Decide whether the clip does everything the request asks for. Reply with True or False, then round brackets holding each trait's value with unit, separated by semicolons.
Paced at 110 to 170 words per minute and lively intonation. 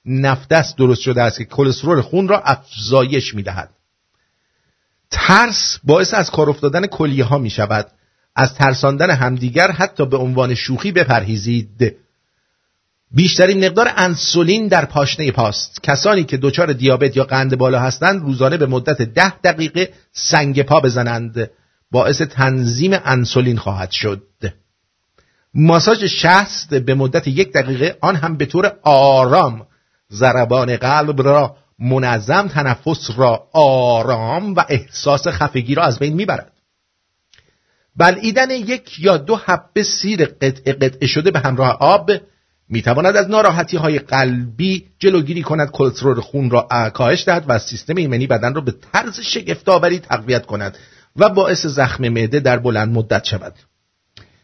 True (135 wpm; 5.9 semitones)